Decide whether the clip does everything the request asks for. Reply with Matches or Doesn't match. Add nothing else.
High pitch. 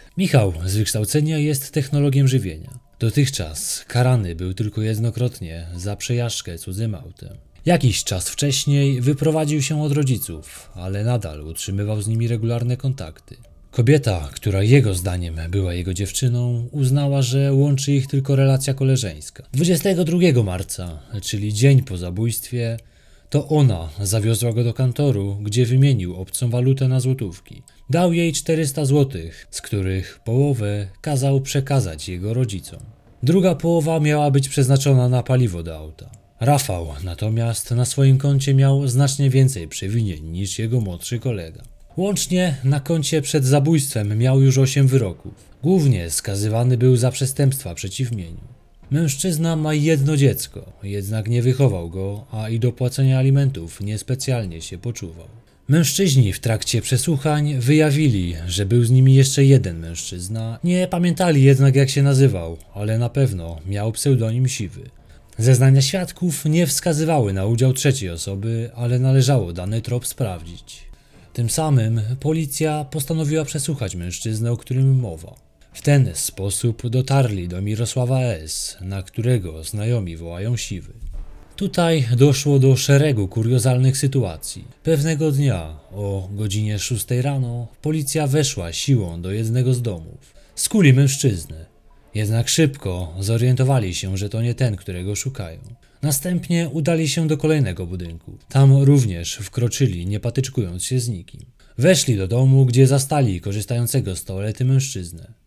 Doesn't match